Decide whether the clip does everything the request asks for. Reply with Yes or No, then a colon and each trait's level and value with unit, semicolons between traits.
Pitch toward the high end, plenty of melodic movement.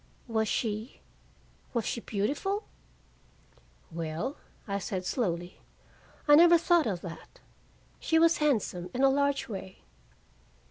Yes: high, 230 Hz; wide, 7.6 semitones